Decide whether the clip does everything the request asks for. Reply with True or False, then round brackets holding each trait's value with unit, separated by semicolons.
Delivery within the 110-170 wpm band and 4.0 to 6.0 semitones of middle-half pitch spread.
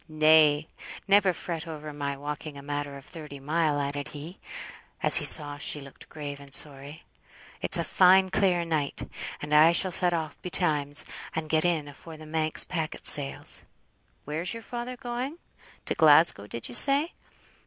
False (165 wpm; 3.1 semitones)